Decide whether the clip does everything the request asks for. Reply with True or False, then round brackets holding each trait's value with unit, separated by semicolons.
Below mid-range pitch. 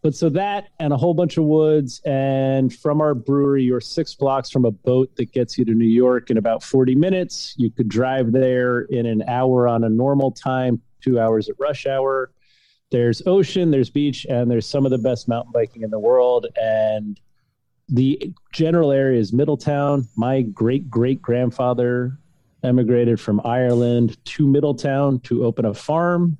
True (130 Hz)